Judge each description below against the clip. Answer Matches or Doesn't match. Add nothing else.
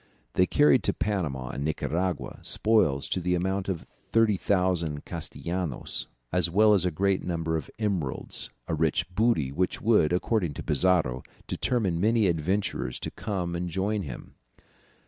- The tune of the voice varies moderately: Matches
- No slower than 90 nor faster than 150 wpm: Matches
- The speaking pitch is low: Matches